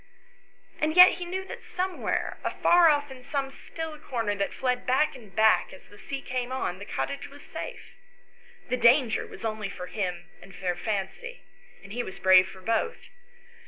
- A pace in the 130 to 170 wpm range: No, average, 180 wpm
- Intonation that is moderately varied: No, wide, 6.7 semitones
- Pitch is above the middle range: Yes, very high, 250 Hz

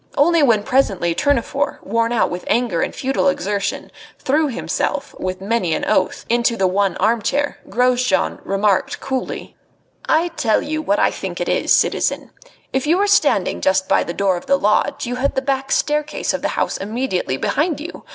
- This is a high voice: Yes, high, 240 Hz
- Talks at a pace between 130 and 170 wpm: No, average, 180 wpm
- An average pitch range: No, wide, 6.2 semitones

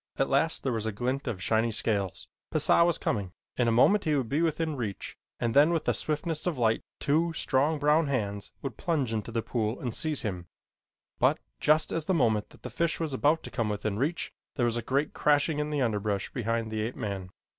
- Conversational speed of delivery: No, fast, 220 wpm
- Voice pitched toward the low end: Yes, low, 130 Hz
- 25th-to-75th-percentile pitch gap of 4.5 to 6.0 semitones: Yes, wide, 5.5 semitones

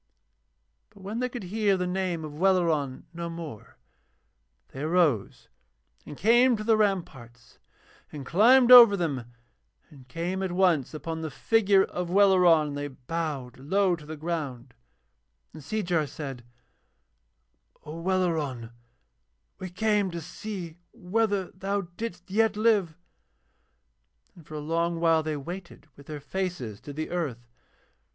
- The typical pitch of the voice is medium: Yes, medium, 170 Hz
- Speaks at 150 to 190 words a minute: No, average, 140 wpm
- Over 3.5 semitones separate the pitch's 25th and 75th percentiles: Yes, average, 4.4 semitones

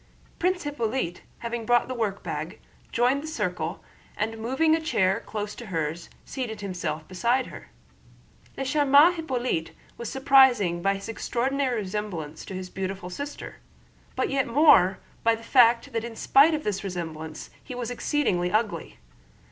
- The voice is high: Yes, high, 225 Hz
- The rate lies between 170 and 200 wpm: No, average, 150 wpm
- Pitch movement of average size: No, wide, 6.2 semitones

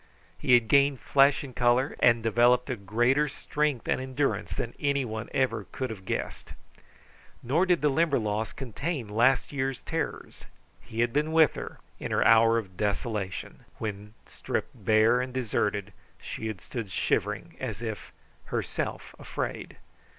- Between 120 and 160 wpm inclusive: Yes, average, 150 wpm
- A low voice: Yes, low, 120 Hz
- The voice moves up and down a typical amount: Yes, average, 3.9 semitones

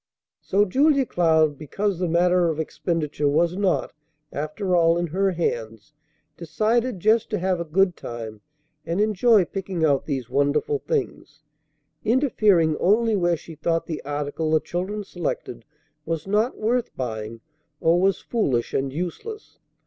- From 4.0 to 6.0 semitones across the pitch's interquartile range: Yes, average, 5.2 semitones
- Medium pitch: Yes, medium, 175 Hz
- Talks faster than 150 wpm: No, average, 145 wpm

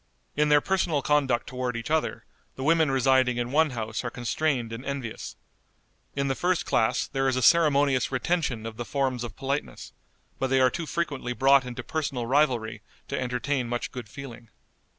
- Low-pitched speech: Yes, low, 130 Hz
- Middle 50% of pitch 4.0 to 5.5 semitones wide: No, average, 3.0 semitones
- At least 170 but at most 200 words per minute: Yes, average, 180 wpm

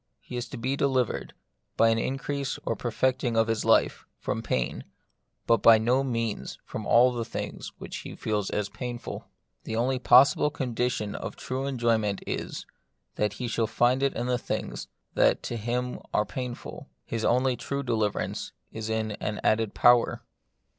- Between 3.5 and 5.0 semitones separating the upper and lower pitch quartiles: No, narrow, 2.4 semitones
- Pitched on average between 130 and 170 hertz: No, low, 120 Hz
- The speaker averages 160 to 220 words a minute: Yes, average, 165 wpm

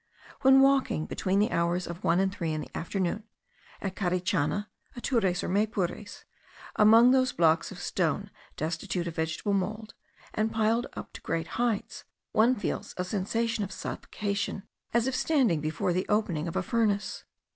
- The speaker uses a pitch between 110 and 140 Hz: No, high, 200 Hz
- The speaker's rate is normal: Yes, average, 160 wpm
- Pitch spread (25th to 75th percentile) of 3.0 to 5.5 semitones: Yes, average, 4.3 semitones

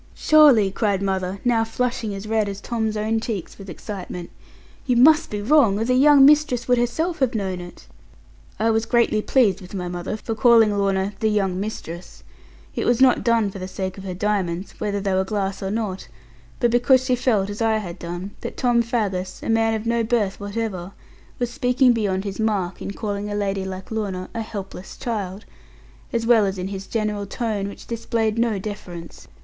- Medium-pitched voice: No, high, 210 Hz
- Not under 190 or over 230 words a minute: Yes, average, 200 wpm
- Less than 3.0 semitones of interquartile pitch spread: No, average, 3.3 semitones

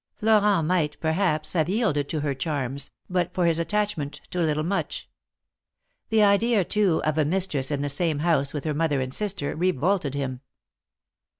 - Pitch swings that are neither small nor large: Yes, average, 4.9 semitones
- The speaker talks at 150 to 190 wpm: Yes, average, 170 wpm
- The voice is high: No, medium, 160 Hz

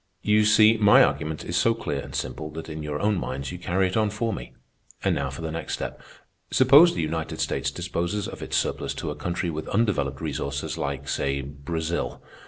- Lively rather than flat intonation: Yes, wide, 6.0 semitones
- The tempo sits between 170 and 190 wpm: No, fast, 205 wpm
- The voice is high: No, very low, 80 Hz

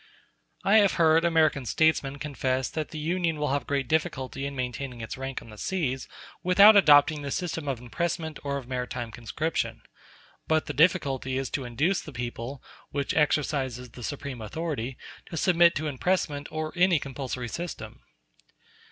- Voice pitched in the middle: Yes, medium, 145 Hz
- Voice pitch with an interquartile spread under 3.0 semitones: No, average, 3.8 semitones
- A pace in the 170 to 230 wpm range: No, average, 160 wpm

